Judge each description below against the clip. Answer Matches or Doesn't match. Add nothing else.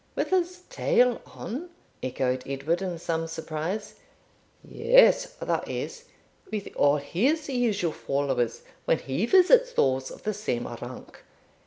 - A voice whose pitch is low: Doesn't match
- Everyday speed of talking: Doesn't match